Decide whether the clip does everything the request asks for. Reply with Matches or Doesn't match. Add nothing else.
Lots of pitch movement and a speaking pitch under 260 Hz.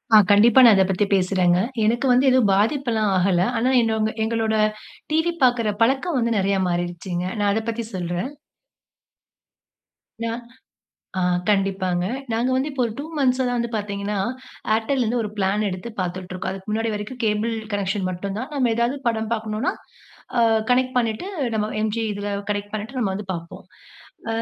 Doesn't match